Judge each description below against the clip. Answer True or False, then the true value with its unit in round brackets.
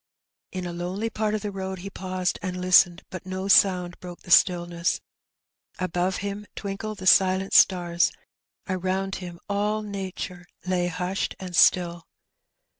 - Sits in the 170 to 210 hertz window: True (185 Hz)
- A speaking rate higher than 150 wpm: False (145 wpm)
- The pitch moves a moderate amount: False (1.6 semitones)